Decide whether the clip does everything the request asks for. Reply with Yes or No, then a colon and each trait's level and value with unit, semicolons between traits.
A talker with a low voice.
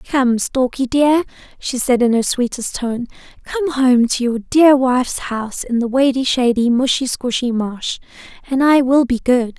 No: very high, 255 Hz